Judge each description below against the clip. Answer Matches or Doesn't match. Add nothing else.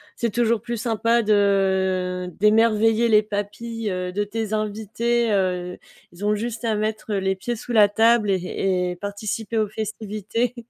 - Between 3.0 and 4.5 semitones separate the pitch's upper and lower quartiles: Doesn't match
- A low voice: Doesn't match